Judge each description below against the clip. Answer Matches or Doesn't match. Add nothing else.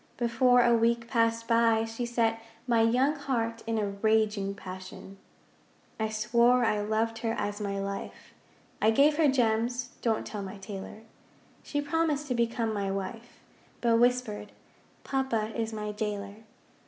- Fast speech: Doesn't match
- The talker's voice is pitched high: Matches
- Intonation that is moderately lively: Doesn't match